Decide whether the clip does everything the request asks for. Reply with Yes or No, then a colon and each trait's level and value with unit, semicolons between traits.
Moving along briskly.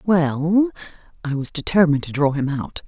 No: average, 165 wpm